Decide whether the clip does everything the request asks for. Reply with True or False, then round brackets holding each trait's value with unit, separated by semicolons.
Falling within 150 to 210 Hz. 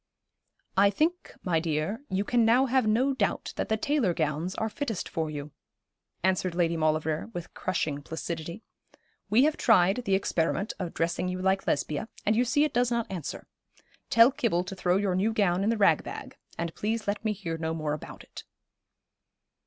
True (190 Hz)